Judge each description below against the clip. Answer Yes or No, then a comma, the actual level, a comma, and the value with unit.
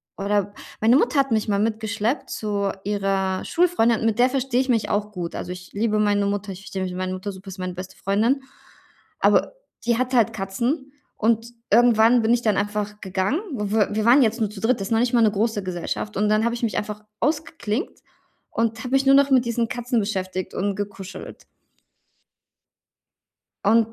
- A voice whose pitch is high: Yes, high, 215 Hz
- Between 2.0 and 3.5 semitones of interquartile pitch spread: Yes, average, 3.0 semitones